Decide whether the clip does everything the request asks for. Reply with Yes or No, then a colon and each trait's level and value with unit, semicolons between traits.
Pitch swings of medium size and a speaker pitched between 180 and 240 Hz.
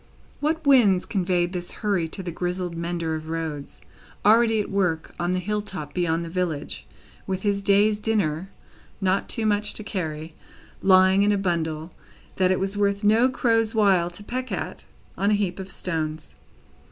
Yes: average, 3.5 semitones; high, 190 Hz